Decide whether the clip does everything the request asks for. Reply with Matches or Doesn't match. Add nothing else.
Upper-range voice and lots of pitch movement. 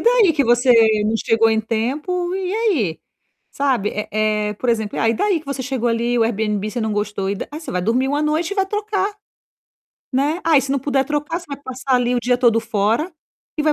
Matches